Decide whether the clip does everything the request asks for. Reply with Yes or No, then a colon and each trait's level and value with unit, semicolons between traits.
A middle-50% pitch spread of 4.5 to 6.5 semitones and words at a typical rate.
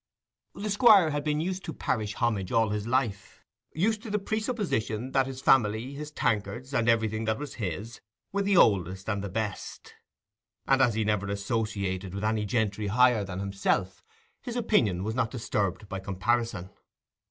Yes: average, 5.2 semitones; average, 165 wpm